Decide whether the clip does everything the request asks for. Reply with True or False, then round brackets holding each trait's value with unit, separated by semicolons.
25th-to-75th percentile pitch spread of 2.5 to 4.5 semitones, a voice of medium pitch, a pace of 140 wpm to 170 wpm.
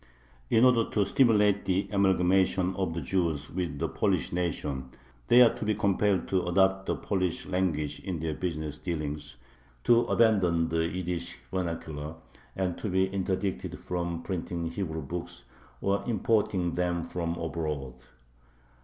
False (2.8 semitones; 90 Hz; 145 wpm)